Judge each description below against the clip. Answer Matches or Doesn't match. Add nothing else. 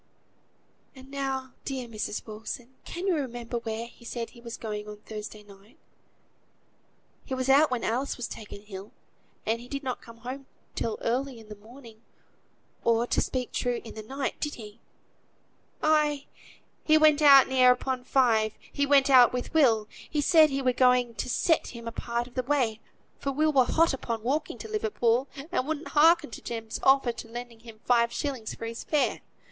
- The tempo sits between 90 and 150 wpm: Doesn't match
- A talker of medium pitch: Doesn't match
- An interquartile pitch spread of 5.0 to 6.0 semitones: Doesn't match